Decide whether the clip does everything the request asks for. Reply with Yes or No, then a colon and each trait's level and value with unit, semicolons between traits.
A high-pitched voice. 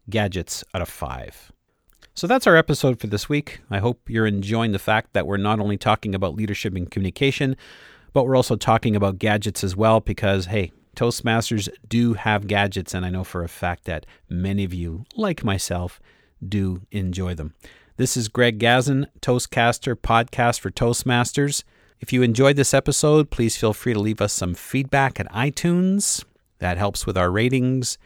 No: low, 110 Hz